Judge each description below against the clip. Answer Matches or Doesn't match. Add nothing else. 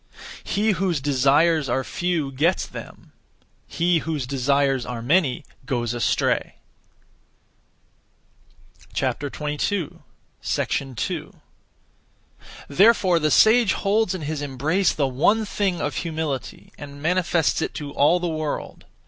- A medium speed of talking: Doesn't match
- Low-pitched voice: Doesn't match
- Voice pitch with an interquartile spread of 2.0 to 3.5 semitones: Doesn't match